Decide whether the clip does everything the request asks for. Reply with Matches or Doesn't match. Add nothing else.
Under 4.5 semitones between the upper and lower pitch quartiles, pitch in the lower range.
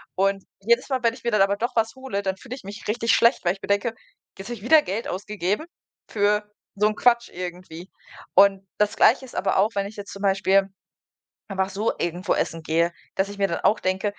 Doesn't match